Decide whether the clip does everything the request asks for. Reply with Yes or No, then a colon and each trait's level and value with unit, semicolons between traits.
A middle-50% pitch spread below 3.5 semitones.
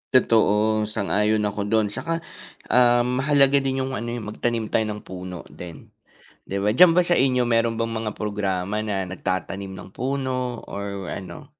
No: average, 4.0 semitones